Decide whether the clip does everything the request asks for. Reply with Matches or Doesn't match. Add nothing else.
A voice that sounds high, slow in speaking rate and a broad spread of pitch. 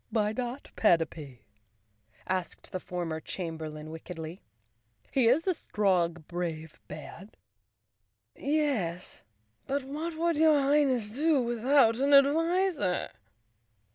Matches